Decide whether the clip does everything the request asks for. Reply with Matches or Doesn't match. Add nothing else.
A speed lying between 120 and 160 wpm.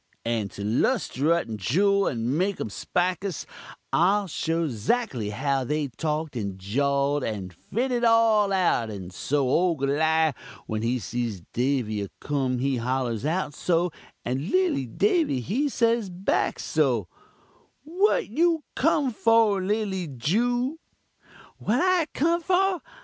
Matches